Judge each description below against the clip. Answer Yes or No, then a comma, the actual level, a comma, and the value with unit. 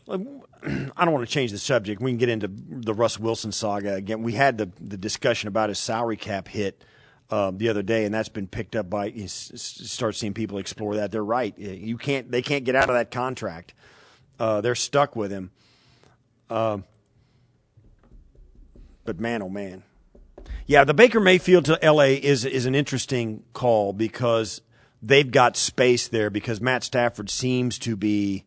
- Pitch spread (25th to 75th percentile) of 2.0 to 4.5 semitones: Yes, average, 3.4 semitones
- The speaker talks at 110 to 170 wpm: No, average, 185 wpm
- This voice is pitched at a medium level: No, low, 115 Hz